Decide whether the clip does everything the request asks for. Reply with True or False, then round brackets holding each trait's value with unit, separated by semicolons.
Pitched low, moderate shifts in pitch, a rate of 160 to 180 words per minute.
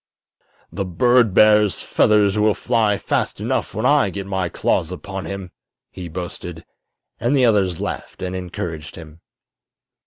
False (95 Hz; 3.2 semitones; 145 wpm)